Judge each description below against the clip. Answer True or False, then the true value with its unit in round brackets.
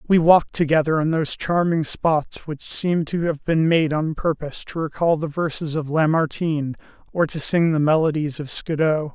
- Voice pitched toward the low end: False (155 Hz)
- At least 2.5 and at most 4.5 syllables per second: False (5.1 syllables/s)